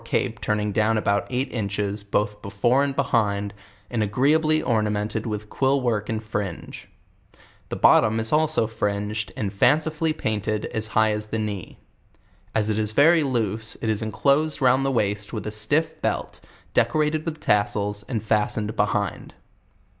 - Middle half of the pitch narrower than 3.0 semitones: No, average, 4.2 semitones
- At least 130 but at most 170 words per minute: Yes, average, 160 wpm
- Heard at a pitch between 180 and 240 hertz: No, low, 110 Hz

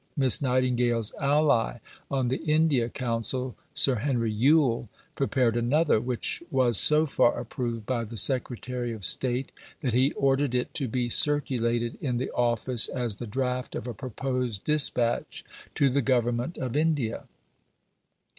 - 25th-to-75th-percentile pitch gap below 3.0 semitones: Yes, narrow, 2.5 semitones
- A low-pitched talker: Yes, low, 125 Hz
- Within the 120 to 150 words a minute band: Yes, average, 145 wpm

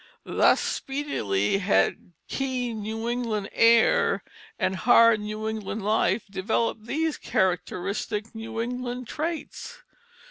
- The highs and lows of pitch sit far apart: No, average, 2.8 semitones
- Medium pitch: No, high, 225 Hz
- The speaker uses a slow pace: Yes, slow, 105 wpm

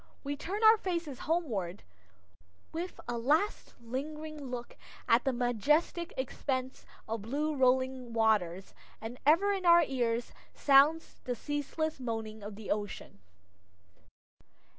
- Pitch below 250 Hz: No, very high, 260 Hz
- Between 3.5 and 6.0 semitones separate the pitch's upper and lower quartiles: Yes, average, 5.3 semitones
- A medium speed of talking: No, slow, 120 wpm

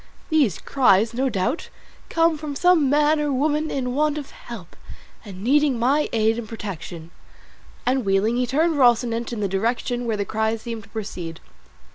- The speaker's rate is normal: Yes, average, 170 wpm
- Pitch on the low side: No, high, 240 Hz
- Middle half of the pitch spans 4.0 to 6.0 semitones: Yes, average, 5.1 semitones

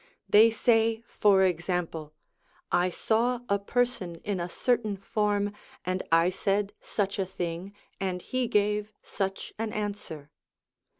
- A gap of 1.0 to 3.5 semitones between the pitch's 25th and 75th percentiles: Yes, average, 2.9 semitones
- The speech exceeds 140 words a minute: No, slow, 135 wpm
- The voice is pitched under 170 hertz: No, high, 200 Hz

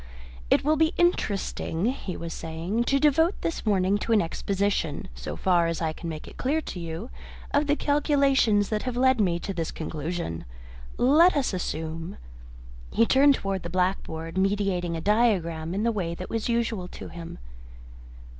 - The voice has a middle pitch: No, high, 195 Hz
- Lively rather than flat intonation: Yes, wide, 6.7 semitones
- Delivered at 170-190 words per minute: Yes, average, 175 wpm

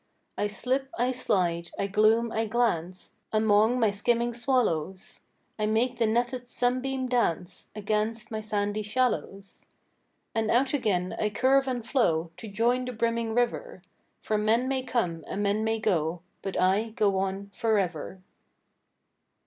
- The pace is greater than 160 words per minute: No, average, 145 wpm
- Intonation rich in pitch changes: No, average, 3.5 semitones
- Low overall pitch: No, high, 220 Hz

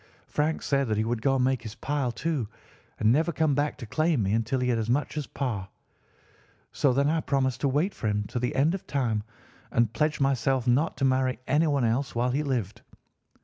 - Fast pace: Yes, fast, 220 wpm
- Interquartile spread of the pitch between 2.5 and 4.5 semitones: Yes, average, 3.8 semitones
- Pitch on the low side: Yes, low, 130 Hz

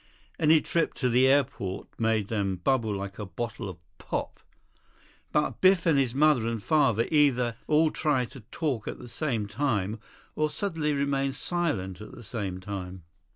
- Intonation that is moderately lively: No, wide, 6.3 semitones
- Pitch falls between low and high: No, low, 125 Hz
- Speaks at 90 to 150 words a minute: No, average, 165 wpm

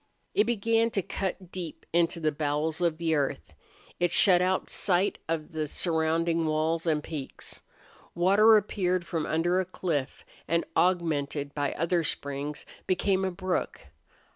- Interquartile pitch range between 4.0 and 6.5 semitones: No, average, 3.1 semitones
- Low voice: No, medium, 170 Hz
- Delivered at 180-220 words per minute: No, average, 145 wpm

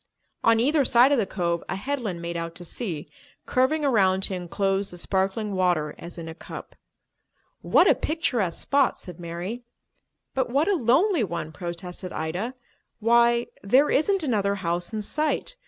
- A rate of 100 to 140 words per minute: No, average, 165 wpm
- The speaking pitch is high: Yes, high, 200 Hz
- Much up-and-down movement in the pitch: Yes, wide, 6.5 semitones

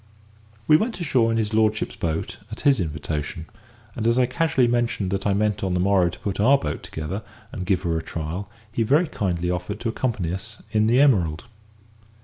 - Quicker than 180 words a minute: Yes, average, 200 wpm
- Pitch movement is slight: No, average, 5.1 semitones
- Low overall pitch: Yes, low, 105 Hz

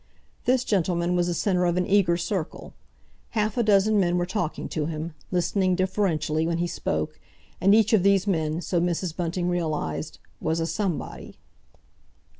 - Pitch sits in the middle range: Yes, medium, 175 Hz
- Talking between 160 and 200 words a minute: Yes, average, 165 wpm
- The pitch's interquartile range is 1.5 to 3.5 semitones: Yes, average, 2.9 semitones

